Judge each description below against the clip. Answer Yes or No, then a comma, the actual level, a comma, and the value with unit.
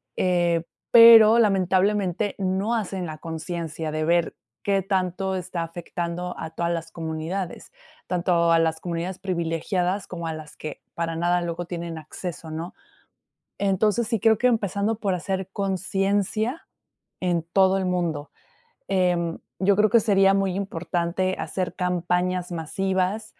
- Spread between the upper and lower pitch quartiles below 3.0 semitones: Yes, narrow, 2.5 semitones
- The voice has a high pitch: No, medium, 180 Hz